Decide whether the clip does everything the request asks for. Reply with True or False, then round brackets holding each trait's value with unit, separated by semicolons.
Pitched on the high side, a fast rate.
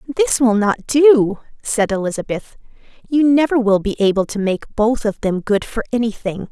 False (225 Hz; 175 wpm)